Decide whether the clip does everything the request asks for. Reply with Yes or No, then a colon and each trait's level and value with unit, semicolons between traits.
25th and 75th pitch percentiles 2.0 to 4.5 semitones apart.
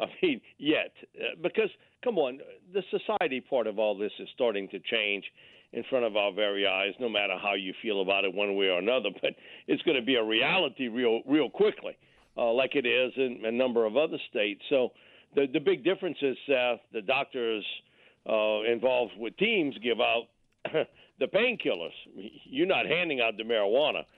No: average, 5.0 semitones